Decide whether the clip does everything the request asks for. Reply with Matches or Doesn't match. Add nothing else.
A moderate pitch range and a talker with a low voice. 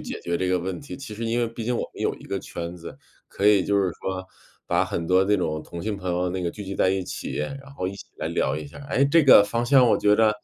Matches